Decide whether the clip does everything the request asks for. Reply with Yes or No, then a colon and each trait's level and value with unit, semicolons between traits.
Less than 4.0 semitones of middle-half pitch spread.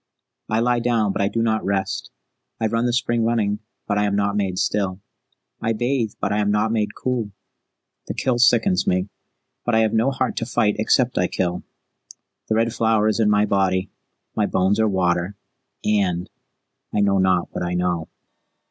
Yes: average, 2.9 semitones